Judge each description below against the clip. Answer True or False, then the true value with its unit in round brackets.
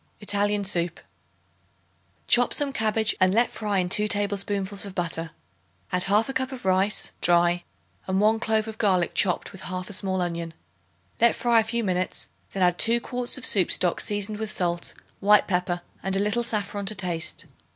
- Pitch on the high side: True (200 Hz)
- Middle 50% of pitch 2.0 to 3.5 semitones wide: True (3.2 semitones)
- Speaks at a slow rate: False (175 wpm)